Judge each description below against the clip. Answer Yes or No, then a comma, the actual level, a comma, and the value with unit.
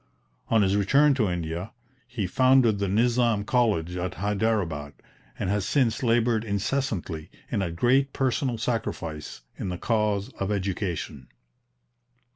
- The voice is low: Yes, low, 105 Hz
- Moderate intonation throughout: Yes, average, 4.6 semitones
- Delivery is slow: Yes, slow, 130 wpm